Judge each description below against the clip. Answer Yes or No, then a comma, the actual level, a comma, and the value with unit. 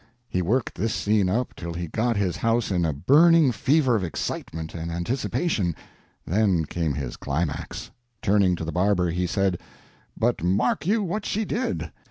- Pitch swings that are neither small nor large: No, wide, 6.0 semitones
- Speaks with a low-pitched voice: Yes, very low, 95 Hz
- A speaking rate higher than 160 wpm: Yes, average, 170 wpm